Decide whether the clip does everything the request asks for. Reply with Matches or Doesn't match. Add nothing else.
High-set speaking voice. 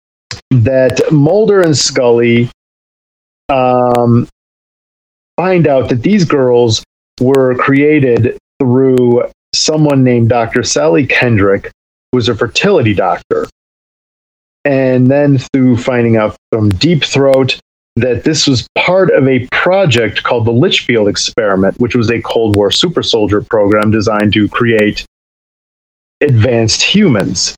Doesn't match